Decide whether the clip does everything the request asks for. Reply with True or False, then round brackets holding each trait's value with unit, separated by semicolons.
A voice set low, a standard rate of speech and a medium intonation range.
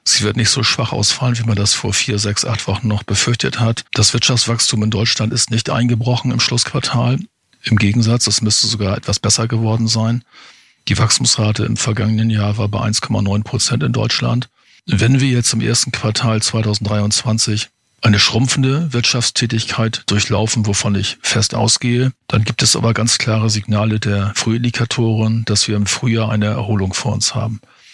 False (115 Hz; 170 wpm; 2.1 semitones)